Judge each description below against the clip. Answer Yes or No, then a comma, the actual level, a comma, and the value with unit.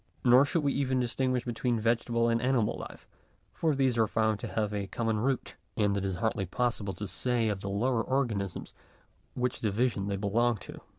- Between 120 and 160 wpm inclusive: No, average, 190 wpm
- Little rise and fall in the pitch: No, average, 3.5 semitones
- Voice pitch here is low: Yes, low, 115 Hz